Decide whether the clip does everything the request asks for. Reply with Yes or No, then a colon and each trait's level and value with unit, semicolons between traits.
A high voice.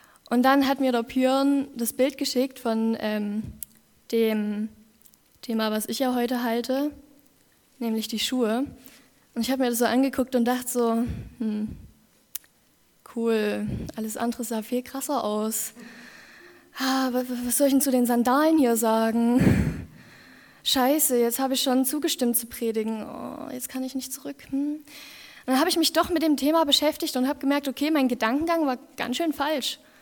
Yes: very high, 255 Hz